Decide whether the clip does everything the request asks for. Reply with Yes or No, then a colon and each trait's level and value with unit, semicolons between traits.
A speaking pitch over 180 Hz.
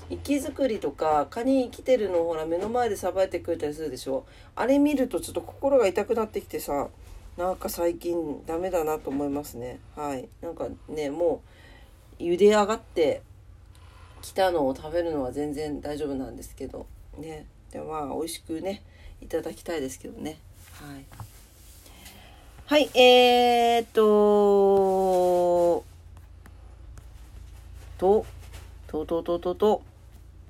No: medium, 150 Hz